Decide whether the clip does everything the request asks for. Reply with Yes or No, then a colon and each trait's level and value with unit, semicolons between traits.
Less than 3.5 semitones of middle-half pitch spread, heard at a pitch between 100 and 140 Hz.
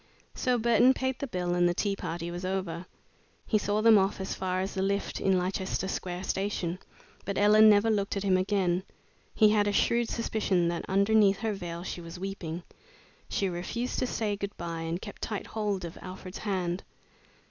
No: average, 2.8 semitones; high, 195 Hz